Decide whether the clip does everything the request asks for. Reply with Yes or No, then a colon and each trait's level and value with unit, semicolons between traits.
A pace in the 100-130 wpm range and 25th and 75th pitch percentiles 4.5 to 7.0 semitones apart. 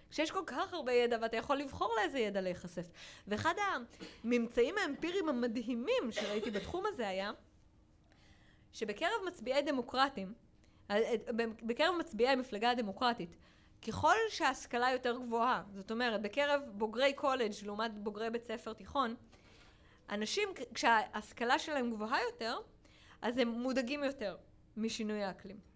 Yes: average, 120 wpm; average, 4.8 semitones